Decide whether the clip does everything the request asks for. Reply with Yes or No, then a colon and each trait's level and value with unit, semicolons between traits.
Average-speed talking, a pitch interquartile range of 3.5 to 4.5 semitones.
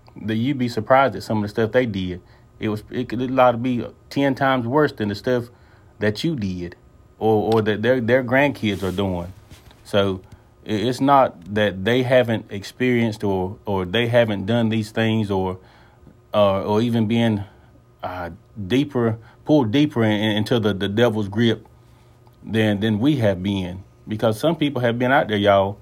No: average, 185 wpm; average, 3.0 semitones